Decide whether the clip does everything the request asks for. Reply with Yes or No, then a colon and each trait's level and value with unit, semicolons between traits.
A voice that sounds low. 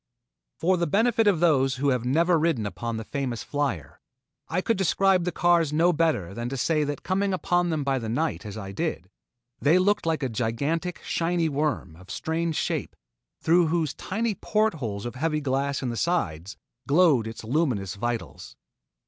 No: medium, 150 Hz